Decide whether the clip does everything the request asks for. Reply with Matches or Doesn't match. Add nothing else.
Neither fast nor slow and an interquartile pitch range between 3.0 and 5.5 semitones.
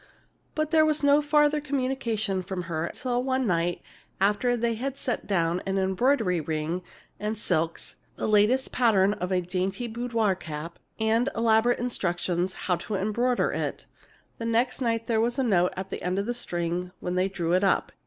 Matches